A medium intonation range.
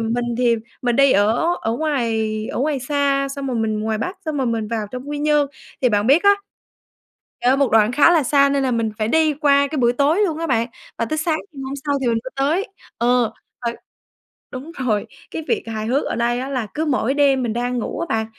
Yes: average, 4.0 semitones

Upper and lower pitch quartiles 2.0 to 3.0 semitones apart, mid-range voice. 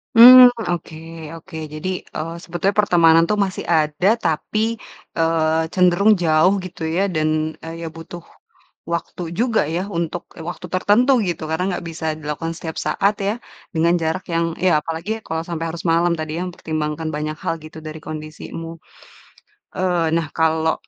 Yes: narrow, 2.4 semitones; medium, 165 Hz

